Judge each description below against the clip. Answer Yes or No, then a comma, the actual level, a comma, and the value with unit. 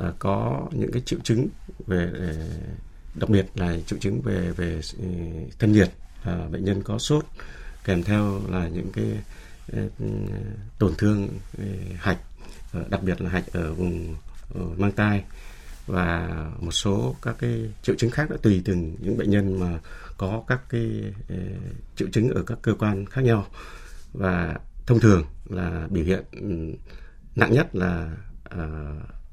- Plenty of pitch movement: No, average, 3.9 semitones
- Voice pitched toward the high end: No, very low, 95 Hz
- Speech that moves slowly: Yes, slow, 160 wpm